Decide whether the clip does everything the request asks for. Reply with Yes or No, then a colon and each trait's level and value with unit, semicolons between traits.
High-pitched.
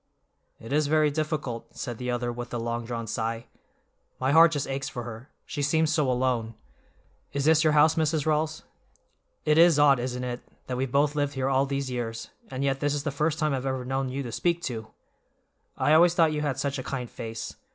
No: low, 135 Hz